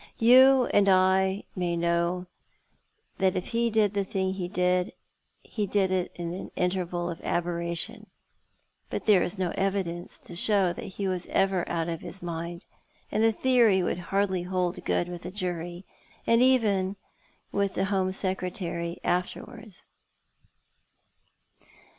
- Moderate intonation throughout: No, narrow, 2.3 semitones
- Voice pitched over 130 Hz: Yes, medium, 185 Hz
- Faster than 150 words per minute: No, average, 140 wpm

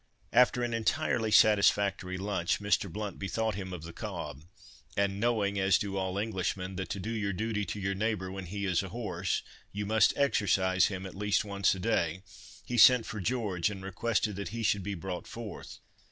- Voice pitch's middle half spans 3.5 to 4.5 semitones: No, narrow, 2.6 semitones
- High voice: No, low, 100 Hz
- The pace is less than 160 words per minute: No, average, 190 wpm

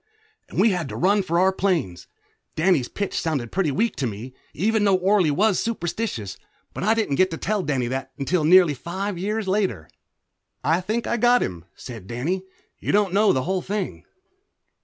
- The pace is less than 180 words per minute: No, average, 185 wpm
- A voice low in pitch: No, medium, 185 Hz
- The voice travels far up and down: Yes, wide, 6.4 semitones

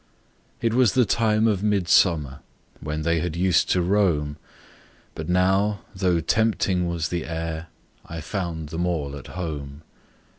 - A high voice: No, very low, 85 Hz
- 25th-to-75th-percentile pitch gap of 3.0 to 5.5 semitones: Yes, average, 3.7 semitones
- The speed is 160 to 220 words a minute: No, average, 145 wpm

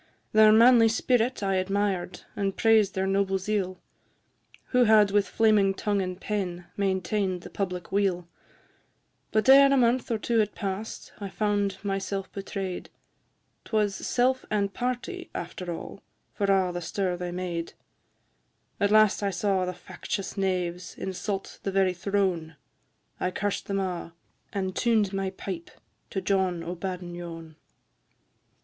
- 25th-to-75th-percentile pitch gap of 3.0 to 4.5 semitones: No, narrow, 2.4 semitones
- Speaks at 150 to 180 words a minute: No, average, 140 wpm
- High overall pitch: Yes, high, 195 Hz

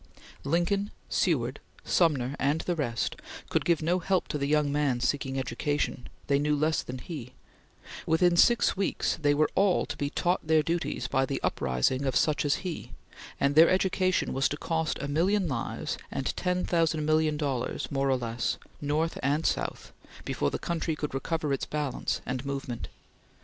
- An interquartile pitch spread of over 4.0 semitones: No, average, 3.4 semitones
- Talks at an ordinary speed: Yes, average, 175 wpm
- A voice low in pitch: No, medium, 150 Hz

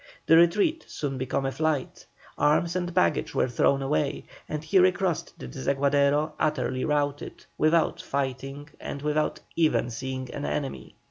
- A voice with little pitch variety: No, average, 3.1 semitones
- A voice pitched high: No, medium, 145 Hz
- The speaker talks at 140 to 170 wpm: Yes, average, 145 wpm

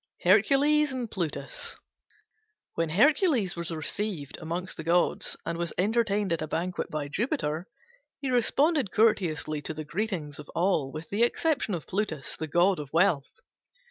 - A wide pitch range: Yes, wide, 6.1 semitones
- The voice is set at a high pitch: No, medium, 180 Hz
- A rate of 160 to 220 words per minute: No, average, 150 wpm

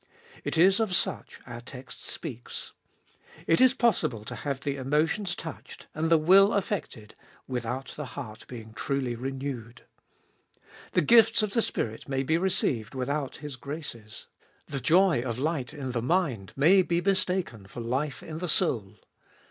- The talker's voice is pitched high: No, medium, 140 Hz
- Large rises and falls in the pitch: Yes, wide, 6.3 semitones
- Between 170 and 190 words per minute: No, average, 155 wpm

